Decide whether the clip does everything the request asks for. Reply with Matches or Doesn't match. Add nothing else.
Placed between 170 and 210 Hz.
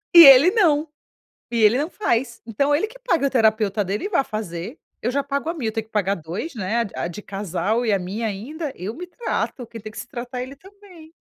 Doesn't match